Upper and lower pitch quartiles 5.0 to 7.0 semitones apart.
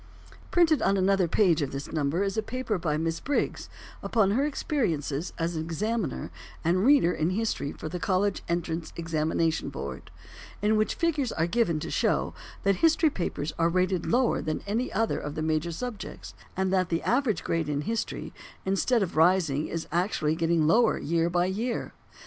Yes: average, 5.3 semitones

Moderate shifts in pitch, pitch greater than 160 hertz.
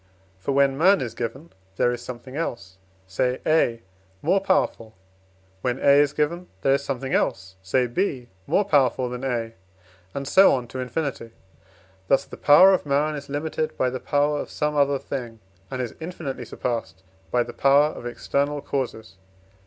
No: average, 3.5 semitones; low, 135 Hz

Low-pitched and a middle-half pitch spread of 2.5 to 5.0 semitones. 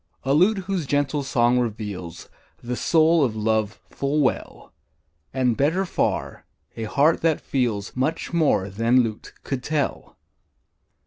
No: low, 130 Hz; wide, 5.4 semitones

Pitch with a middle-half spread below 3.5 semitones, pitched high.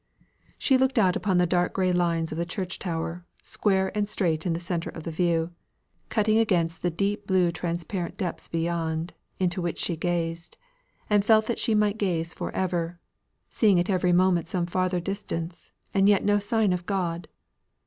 No: average, 2.8 semitones; medium, 180 Hz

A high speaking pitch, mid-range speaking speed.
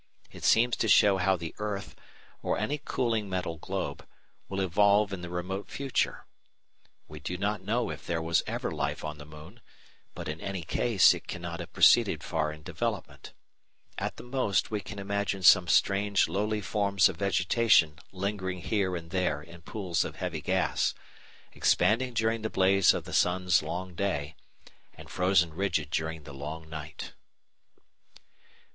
No: very low, 95 Hz; average, 165 wpm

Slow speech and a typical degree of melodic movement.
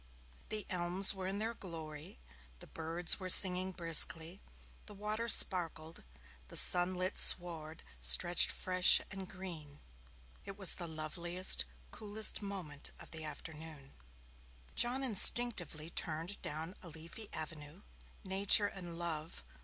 Yes: slow, 120 wpm; average, 3.4 semitones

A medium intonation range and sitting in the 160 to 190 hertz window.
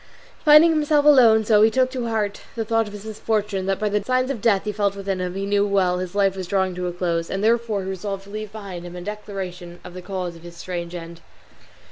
No: average, 3.2 semitones; high, 200 Hz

